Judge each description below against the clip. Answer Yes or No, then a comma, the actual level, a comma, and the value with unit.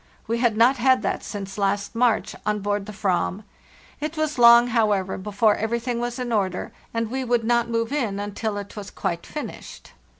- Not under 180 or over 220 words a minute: Yes, average, 190 wpm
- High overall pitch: Yes, high, 225 Hz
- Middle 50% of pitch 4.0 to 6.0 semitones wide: No, average, 2.9 semitones